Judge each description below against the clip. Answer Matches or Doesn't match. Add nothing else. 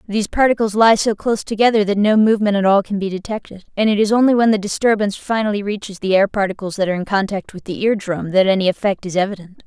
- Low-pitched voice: Doesn't match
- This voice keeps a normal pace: Doesn't match